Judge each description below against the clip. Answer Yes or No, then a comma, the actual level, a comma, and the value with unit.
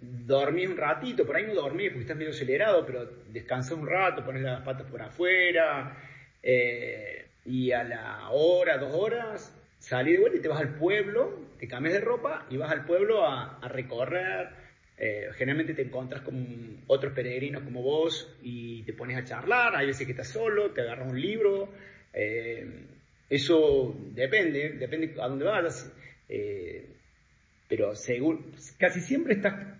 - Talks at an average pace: Yes, average, 165 wpm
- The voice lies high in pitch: No, medium, 155 Hz